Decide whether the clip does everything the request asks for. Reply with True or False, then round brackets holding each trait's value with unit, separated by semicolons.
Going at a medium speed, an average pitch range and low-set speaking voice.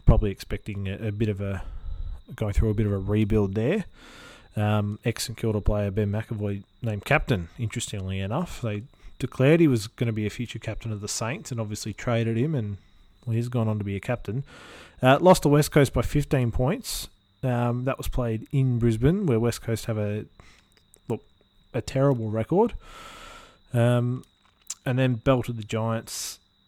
True (180 wpm; 3.6 semitones; 115 Hz)